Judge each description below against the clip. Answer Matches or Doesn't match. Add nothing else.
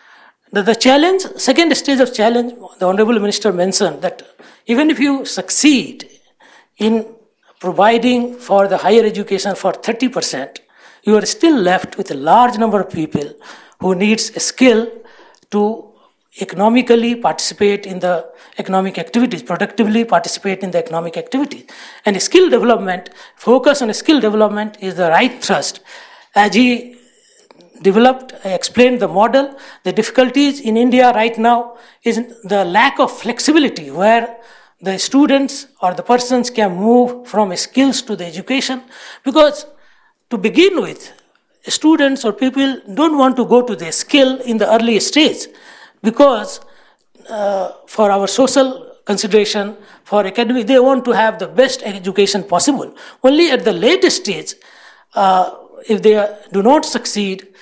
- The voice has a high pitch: Matches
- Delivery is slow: Doesn't match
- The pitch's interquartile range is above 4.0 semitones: Matches